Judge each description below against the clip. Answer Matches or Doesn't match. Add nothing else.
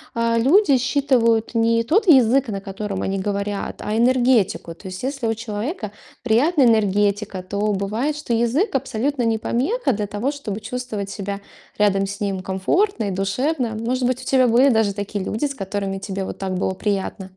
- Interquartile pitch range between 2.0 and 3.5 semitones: Doesn't match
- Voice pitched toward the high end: Matches